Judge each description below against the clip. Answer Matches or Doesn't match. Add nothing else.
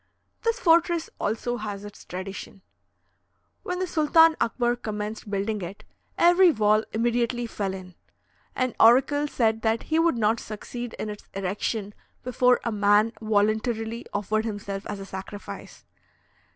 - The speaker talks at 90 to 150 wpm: Matches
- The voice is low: Doesn't match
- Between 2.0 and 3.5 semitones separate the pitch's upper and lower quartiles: Matches